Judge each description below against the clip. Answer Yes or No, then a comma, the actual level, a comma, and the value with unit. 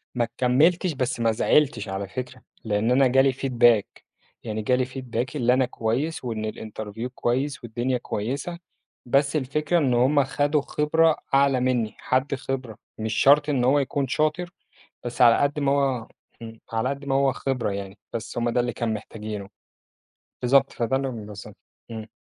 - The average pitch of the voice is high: No, low, 125 Hz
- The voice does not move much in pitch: No, average, 3.3 semitones